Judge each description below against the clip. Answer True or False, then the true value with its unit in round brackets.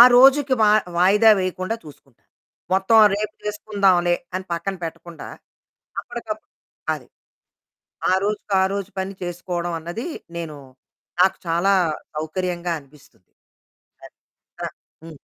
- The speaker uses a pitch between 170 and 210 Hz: True (185 Hz)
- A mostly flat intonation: False (3.5 semitones)